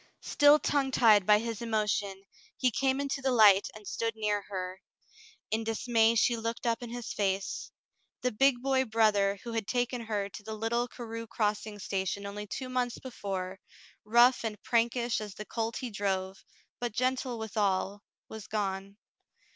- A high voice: Yes, high, 220 Hz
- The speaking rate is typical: Yes, average, 170 wpm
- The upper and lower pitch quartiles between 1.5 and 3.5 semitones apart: Yes, average, 2.9 semitones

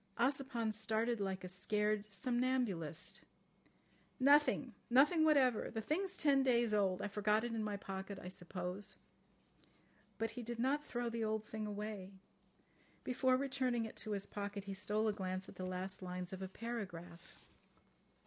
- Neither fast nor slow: Yes, average, 160 wpm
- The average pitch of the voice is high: Yes, high, 215 Hz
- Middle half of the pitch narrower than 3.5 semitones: No, average, 4.1 semitones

